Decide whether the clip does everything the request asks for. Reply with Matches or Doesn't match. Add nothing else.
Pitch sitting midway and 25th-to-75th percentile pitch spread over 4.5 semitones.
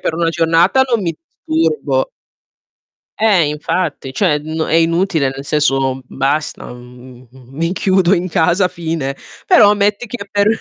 Matches